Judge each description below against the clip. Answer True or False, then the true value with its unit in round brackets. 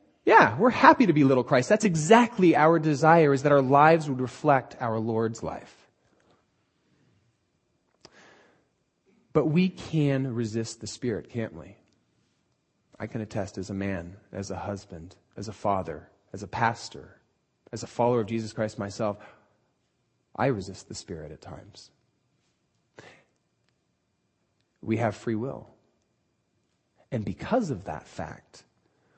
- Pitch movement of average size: False (6.0 semitones)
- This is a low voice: True (115 Hz)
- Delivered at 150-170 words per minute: False (135 wpm)